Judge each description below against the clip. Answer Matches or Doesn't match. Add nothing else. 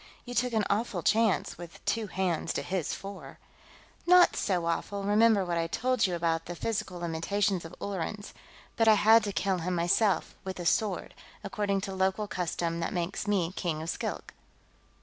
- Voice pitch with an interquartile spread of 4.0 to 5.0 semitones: Doesn't match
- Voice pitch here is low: Doesn't match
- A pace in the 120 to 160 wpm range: Doesn't match